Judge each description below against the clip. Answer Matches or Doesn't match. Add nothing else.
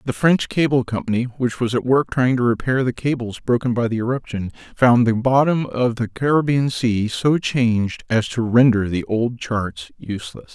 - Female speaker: Doesn't match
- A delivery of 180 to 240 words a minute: Matches